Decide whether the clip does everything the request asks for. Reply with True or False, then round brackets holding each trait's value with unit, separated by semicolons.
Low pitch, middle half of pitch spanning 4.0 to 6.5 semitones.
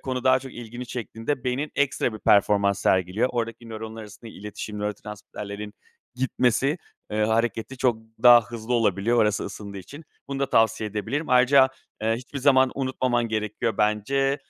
False (115 Hz; 3.4 semitones)